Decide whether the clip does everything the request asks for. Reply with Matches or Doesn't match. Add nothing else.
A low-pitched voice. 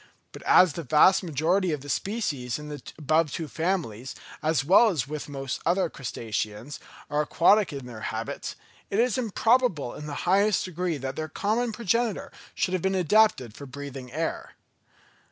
Doesn't match